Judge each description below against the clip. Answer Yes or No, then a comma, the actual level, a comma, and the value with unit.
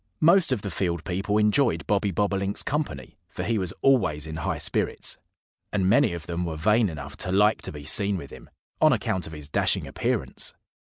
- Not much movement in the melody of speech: No, average, 4.2 semitones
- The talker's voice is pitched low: Yes, low, 100 Hz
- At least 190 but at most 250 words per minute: Yes, average, 195 wpm